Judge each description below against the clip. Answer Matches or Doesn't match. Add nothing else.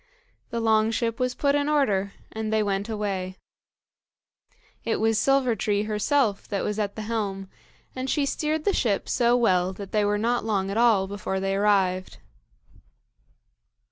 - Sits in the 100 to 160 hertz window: Doesn't match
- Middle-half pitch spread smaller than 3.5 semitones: Matches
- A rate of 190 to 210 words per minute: Doesn't match